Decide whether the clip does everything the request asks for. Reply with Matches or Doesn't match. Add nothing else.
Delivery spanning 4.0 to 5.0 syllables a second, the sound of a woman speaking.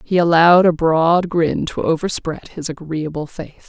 Matches